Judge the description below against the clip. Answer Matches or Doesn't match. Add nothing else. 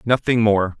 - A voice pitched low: Matches